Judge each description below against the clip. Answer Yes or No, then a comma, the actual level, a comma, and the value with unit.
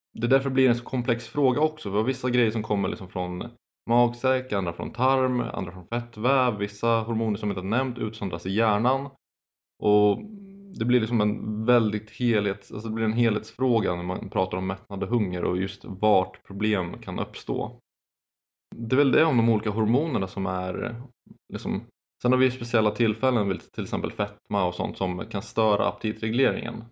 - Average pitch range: Yes, average, 3.4 semitones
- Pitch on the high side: No, low, 110 Hz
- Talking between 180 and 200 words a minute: Yes, average, 190 wpm